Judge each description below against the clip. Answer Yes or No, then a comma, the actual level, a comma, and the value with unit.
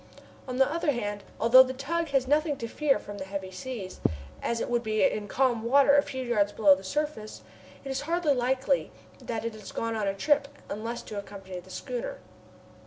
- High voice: Yes, high, 240 Hz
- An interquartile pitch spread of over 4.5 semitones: Yes, average, 5.2 semitones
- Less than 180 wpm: No, fast, 205 wpm